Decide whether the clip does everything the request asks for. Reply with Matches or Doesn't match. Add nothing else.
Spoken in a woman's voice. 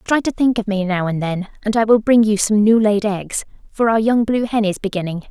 Matches